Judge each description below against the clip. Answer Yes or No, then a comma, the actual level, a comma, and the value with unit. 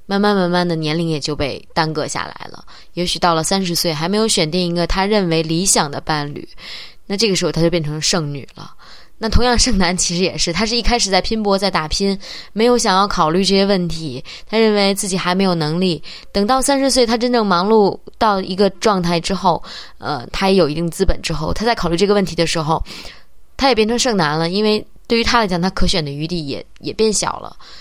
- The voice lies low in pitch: No, medium, 185 Hz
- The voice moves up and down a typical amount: Yes, average, 4.1 semitones